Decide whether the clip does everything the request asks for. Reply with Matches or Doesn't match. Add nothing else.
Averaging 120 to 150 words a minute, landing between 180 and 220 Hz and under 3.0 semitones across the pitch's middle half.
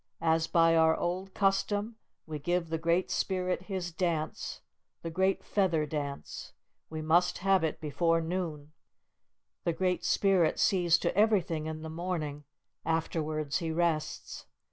Doesn't match